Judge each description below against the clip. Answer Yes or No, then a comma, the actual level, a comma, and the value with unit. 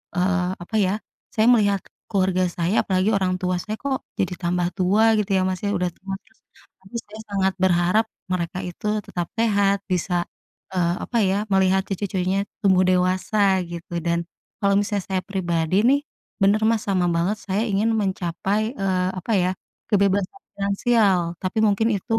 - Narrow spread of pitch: Yes, narrow, 2.0 semitones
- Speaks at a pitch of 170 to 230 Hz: Yes, high, 190 Hz